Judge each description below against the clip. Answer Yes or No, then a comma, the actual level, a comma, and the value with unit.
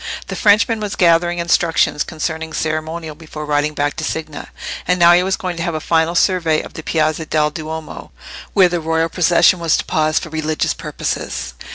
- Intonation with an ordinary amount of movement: No, narrow, 1.8 semitones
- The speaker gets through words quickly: No, average, 190 wpm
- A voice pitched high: No, medium, 160 Hz